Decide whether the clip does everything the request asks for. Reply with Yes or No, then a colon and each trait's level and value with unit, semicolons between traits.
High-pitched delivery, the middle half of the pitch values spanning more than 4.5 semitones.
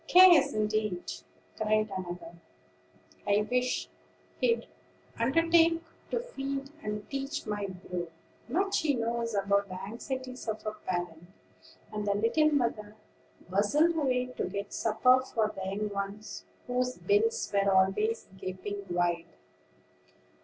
Yes: high, 215 Hz; average, 5.2 semitones